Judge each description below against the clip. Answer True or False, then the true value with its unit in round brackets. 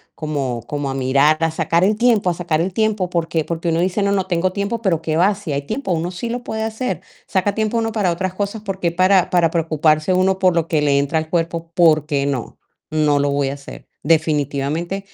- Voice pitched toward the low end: False (170 Hz)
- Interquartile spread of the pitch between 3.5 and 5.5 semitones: True (3.9 semitones)